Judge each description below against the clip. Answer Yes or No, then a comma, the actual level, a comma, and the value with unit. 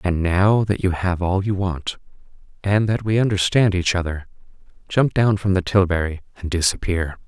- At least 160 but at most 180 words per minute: Yes, average, 175 wpm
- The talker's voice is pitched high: No, very low, 95 Hz